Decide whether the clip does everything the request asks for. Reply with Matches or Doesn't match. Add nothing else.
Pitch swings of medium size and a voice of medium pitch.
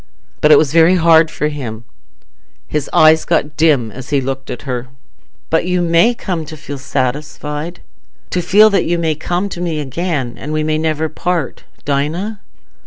Matches